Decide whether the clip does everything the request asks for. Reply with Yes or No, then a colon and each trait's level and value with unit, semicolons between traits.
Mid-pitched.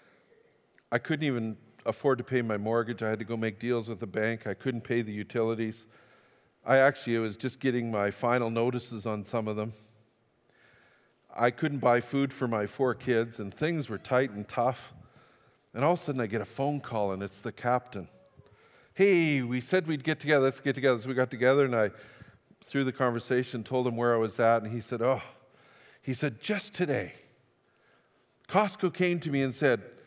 No: low, 120 Hz